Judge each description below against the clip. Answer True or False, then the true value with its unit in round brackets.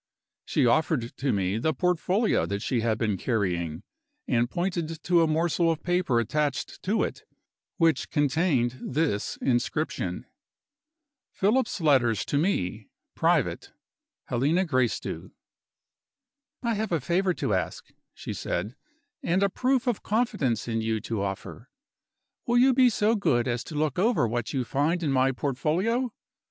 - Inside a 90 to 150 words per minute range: True (145 wpm)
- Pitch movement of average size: False (7.4 semitones)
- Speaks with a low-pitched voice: False (150 Hz)